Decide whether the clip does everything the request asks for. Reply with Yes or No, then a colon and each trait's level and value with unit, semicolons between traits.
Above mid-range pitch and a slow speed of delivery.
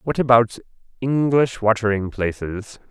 No: low, 115 Hz; slow, 85 wpm